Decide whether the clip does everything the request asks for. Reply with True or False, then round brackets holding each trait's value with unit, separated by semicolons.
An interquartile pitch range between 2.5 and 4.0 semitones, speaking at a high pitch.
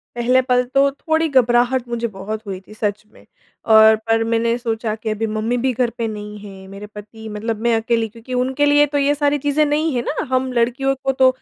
True (3.2 semitones; 235 Hz)